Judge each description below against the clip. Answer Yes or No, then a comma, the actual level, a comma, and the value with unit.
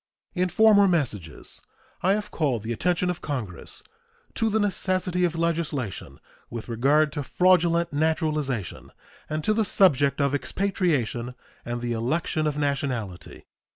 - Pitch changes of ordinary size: No, wide, 6.4 semitones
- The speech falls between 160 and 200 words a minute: No, slow, 135 wpm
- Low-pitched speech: No, medium, 155 Hz